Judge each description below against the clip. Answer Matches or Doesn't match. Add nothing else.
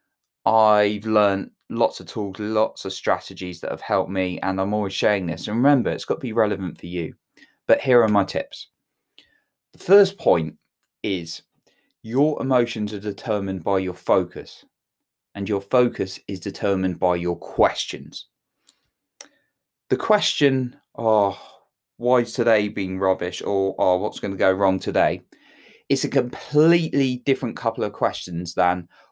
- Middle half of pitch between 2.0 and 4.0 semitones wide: Doesn't match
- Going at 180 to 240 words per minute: Doesn't match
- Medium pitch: Doesn't match